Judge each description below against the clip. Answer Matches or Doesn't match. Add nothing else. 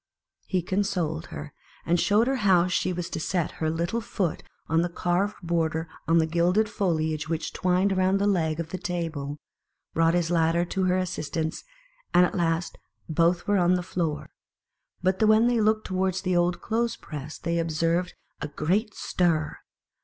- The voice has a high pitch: Doesn't match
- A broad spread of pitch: Doesn't match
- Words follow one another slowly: Doesn't match